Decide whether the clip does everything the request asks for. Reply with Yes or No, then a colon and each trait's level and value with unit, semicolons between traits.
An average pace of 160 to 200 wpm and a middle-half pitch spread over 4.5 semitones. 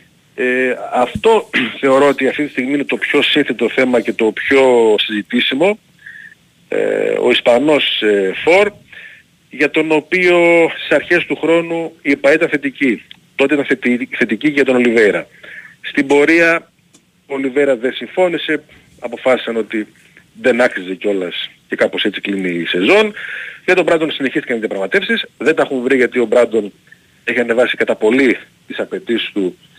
No: average, 150 wpm; average, 5.2 semitones